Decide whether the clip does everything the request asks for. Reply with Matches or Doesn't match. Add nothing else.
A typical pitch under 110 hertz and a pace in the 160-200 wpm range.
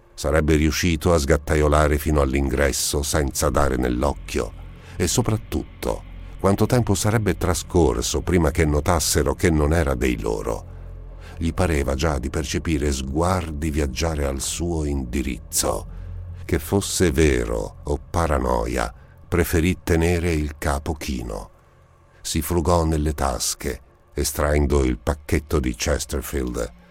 Doesn't match